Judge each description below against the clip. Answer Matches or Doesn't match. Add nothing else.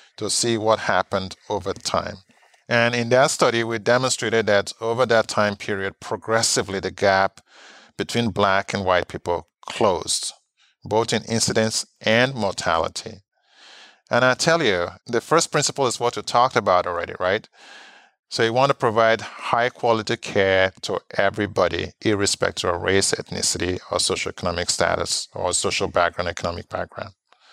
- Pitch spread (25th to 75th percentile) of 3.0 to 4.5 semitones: Matches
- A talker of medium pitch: Doesn't match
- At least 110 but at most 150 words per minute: Matches